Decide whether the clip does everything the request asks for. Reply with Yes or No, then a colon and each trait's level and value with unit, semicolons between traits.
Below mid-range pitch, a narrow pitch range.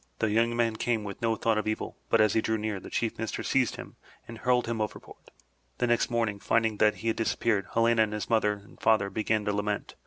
Yes: low, 110 Hz; narrow, 1.5 semitones